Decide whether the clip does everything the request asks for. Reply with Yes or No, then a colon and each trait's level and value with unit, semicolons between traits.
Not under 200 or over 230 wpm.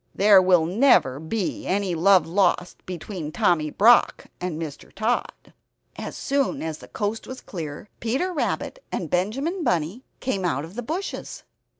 No: average, 155 wpm